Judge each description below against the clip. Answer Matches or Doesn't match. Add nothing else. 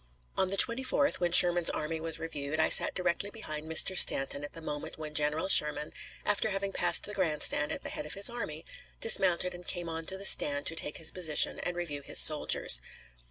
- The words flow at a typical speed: Doesn't match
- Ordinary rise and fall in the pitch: Matches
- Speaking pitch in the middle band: Matches